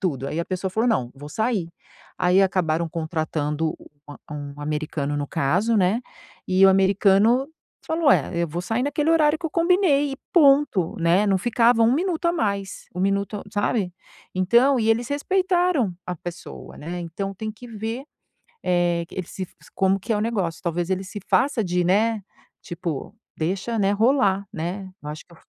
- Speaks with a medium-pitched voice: No, high, 195 Hz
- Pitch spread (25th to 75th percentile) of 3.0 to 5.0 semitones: No, wide, 5.5 semitones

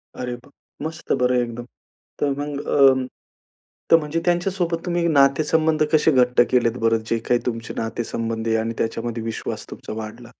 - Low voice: Yes, low, 125 Hz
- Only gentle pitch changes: No, average, 5.1 semitones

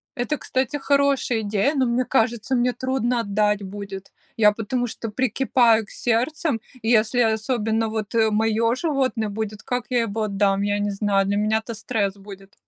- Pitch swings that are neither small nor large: Yes, average, 3.1 semitones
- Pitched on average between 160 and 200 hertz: No, high, 225 Hz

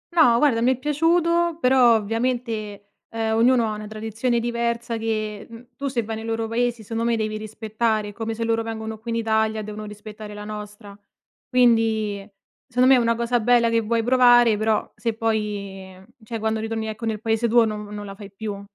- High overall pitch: Yes, high, 225 Hz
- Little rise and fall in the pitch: Yes, narrow, 1.7 semitones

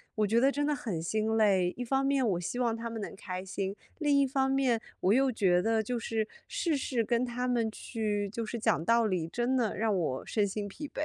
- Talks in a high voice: Yes, high, 225 Hz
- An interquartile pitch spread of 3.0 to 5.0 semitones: Yes, average, 3.8 semitones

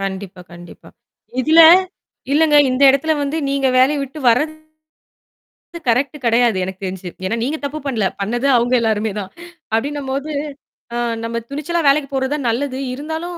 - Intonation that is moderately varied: Yes, average, 4.5 semitones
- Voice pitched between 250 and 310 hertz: Yes, very high, 265 Hz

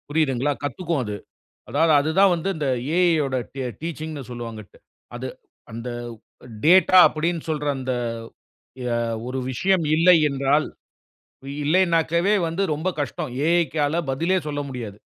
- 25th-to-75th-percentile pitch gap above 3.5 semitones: Yes, average, 4.0 semitones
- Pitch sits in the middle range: Yes, medium, 155 Hz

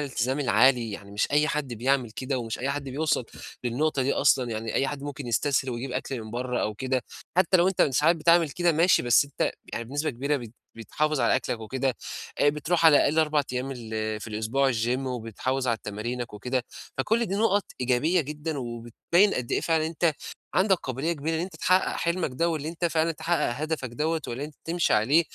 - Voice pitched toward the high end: No, low, 135 Hz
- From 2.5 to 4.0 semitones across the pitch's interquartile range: No, average, 4.7 semitones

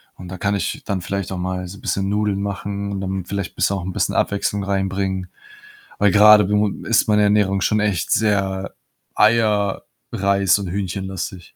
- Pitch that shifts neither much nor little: No, narrow, 1.3 semitones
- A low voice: Yes, low, 100 Hz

